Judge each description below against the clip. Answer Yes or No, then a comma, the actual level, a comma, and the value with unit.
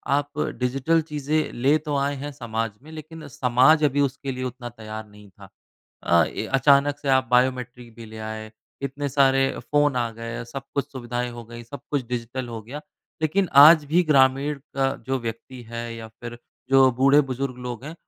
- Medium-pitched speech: No, low, 130 Hz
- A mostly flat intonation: No, average, 3.3 semitones